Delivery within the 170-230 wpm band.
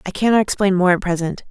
No: fast, 240 wpm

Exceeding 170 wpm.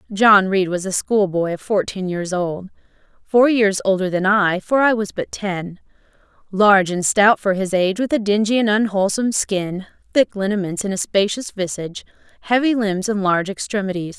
Yes: average, 180 wpm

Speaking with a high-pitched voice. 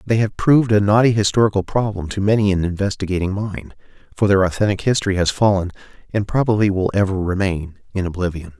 No: low, 100 Hz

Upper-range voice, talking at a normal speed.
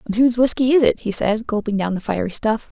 No: high, 225 Hz; fast, 255 wpm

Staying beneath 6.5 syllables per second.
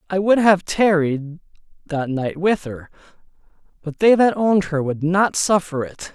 Yes: 4.0 syllables/s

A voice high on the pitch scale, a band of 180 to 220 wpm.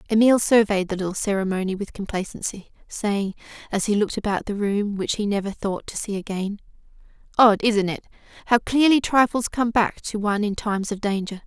Yes: high, 210 Hz; average, 185 wpm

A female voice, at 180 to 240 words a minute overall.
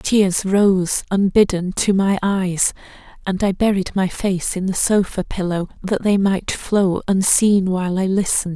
No: female; average, 160 wpm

